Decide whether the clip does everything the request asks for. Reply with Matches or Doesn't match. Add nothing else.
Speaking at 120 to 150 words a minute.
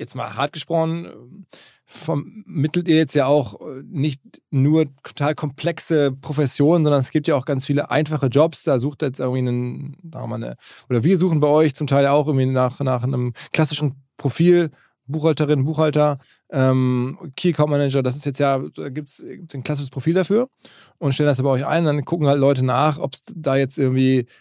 Doesn't match